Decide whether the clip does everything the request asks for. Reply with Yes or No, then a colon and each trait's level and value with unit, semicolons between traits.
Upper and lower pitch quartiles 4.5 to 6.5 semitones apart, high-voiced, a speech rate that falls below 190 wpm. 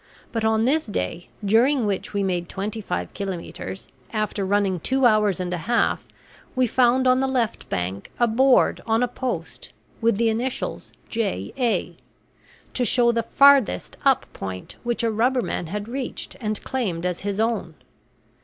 No: average, 4.1 semitones; high, 220 Hz; average, 165 wpm